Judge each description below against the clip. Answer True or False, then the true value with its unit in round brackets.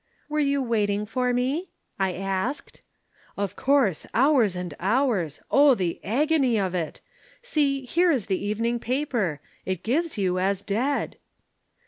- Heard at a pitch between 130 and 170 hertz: False (230 Hz)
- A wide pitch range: True (6.3 semitones)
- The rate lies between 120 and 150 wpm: True (140 wpm)